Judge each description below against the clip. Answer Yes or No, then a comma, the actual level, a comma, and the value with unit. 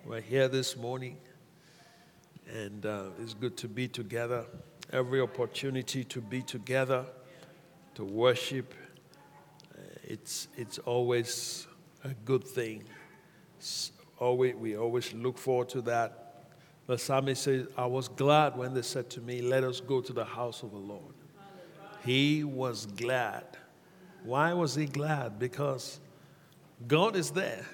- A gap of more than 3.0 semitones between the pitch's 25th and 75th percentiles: Yes, average, 3.6 semitones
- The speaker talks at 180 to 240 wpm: No, slow, 135 wpm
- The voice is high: No, low, 130 Hz